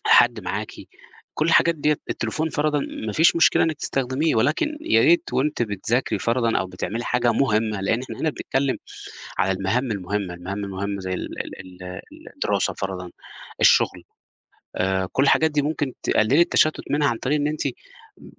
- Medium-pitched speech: No, low, 120 Hz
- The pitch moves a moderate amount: No, wide, 7.3 semitones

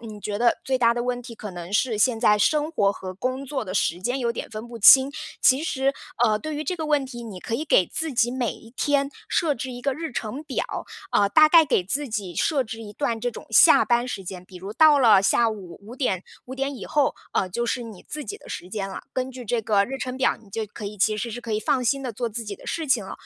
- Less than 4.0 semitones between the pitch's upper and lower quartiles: No, average, 4.3 semitones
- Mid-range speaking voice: No, high, 240 Hz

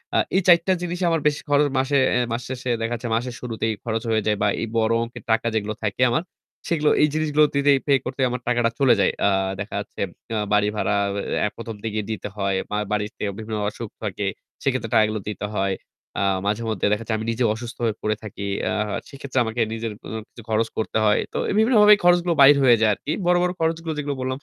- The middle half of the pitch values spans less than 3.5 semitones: No, average, 4.8 semitones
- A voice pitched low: Yes, low, 115 Hz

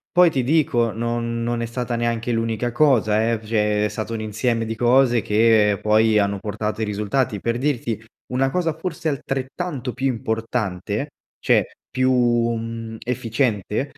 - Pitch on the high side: No, low, 115 Hz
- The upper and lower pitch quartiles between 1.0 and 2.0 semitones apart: No, narrow, 2.6 semitones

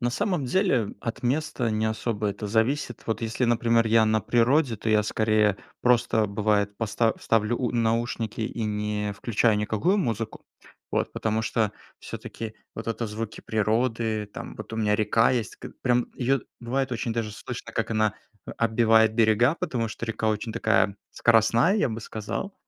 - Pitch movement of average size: No, narrow, 1.8 semitones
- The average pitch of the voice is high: No, low, 115 Hz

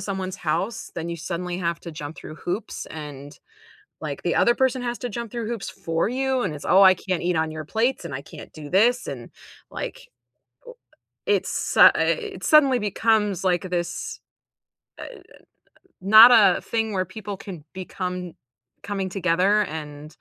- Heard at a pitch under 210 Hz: Yes, high, 190 Hz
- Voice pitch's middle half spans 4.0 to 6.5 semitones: Yes, average, 5.0 semitones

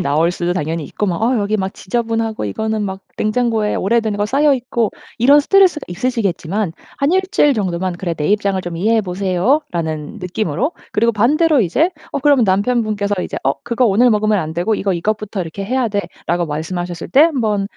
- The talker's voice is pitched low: No, high, 210 Hz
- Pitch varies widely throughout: No, average, 4.9 semitones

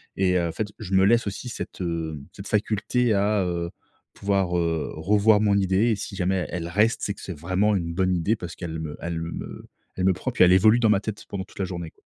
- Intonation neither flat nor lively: Yes, average, 3.2 semitones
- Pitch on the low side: Yes, very low, 95 Hz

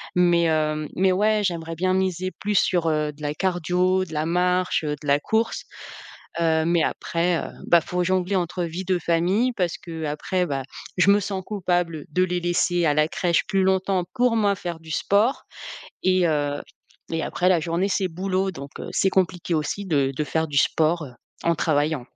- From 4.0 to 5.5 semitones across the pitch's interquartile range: No, average, 2.8 semitones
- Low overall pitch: No, medium, 175 Hz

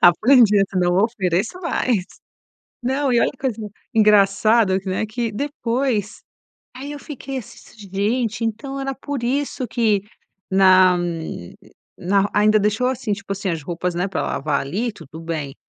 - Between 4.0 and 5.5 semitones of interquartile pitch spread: Yes, average, 4.9 semitones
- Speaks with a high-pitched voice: Yes, high, 215 Hz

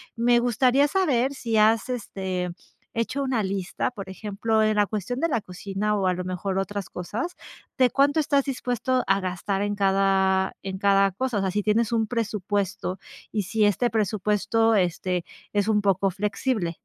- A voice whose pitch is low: No, high, 210 Hz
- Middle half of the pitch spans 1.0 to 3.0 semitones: No, average, 3.5 semitones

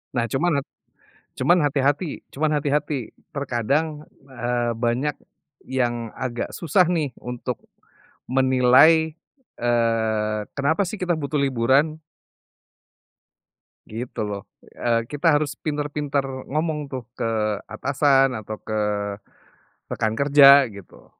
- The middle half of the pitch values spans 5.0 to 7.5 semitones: No, average, 3.8 semitones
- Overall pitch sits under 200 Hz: Yes, low, 135 Hz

